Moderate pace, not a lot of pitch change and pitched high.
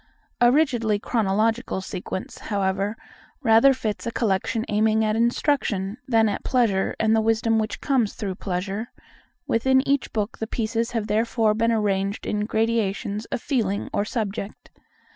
Yes: average, 145 wpm; narrow, 2.3 semitones; high, 220 Hz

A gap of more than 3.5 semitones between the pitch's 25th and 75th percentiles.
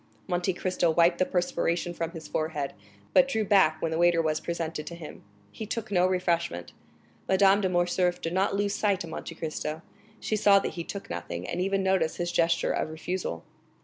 No: narrow, 2.6 semitones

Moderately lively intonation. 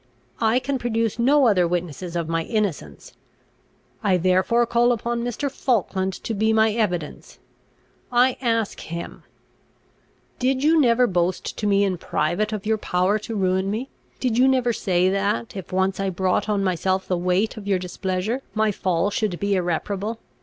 Yes: average, 4.1 semitones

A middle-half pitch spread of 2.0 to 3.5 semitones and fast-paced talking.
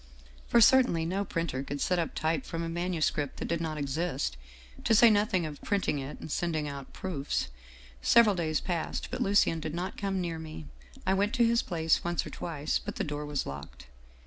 No: average, 4.3 semitones; fast, 215 wpm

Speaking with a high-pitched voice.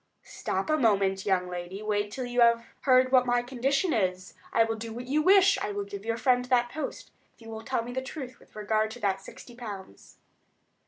Yes: high, 230 Hz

